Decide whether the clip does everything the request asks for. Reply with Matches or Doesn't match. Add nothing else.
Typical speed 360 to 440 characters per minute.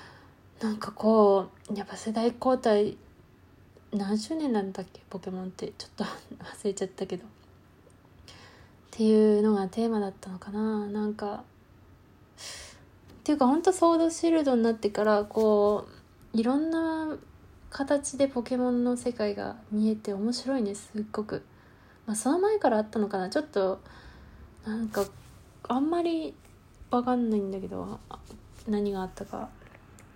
Doesn't match